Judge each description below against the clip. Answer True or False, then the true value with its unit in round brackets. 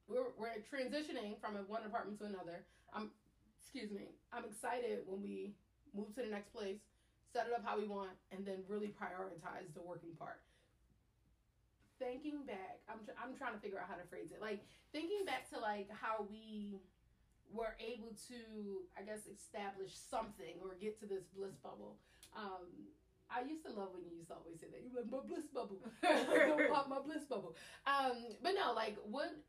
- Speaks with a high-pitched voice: True (215 Hz)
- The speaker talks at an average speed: True (190 wpm)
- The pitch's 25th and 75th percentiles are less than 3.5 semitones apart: False (4.2 semitones)